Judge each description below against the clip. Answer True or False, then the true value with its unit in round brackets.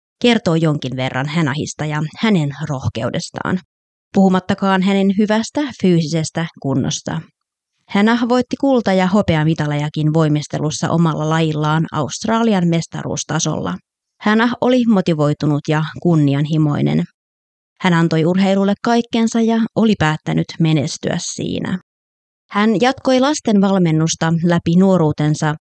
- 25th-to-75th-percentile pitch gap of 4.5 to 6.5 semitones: True (5.0 semitones)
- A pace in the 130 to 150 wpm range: False (100 wpm)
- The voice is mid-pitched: True (165 Hz)